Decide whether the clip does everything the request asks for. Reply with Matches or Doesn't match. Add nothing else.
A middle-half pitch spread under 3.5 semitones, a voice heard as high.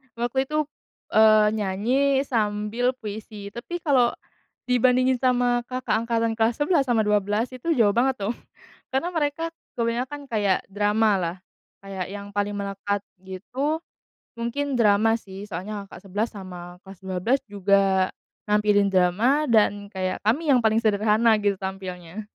Doesn't match